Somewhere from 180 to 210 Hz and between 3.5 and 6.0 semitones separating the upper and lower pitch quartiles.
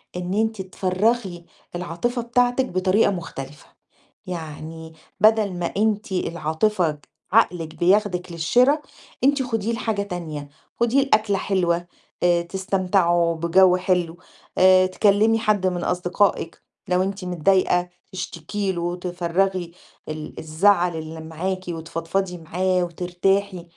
No: medium, 185 Hz; average, 2.9 semitones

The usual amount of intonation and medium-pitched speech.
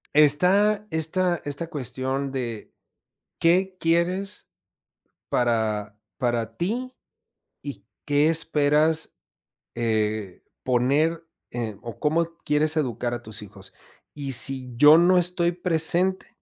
No: wide, 5.9 semitones; medium, 150 Hz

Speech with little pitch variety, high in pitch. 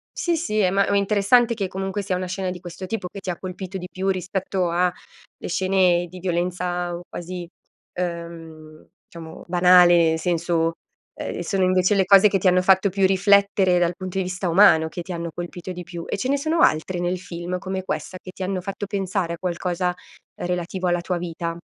No: narrow, 1.7 semitones; medium, 180 Hz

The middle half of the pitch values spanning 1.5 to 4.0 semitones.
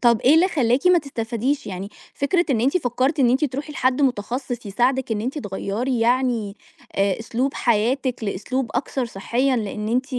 Yes: average, 3.3 semitones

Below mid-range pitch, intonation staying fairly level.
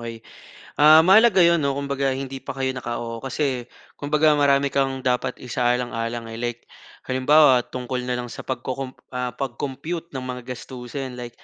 Yes: low, 130 Hz; narrow, 2.3 semitones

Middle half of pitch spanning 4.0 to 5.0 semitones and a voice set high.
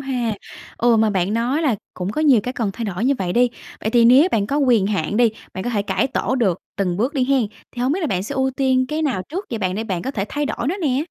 Yes: average, 4.7 semitones; high, 240 Hz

